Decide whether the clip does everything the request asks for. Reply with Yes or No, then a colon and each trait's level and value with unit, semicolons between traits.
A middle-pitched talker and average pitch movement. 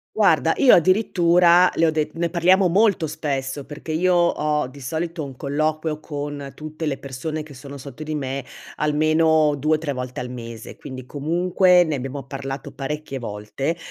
Yes: medium, 150 Hz; average, 3.2 semitones